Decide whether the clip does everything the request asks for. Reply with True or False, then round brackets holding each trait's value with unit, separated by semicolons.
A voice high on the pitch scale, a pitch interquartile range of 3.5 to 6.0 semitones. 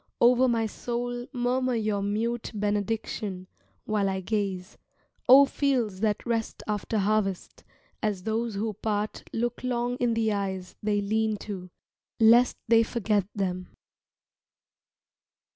False (220 Hz; 2.8 semitones)